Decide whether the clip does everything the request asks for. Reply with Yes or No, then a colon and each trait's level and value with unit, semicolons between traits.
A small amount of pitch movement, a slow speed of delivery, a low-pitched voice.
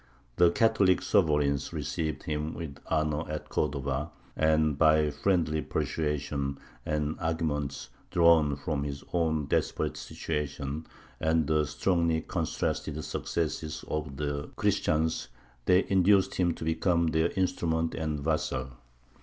Yes: narrow, 1.9 semitones; slow, 120 wpm; very low, 80 Hz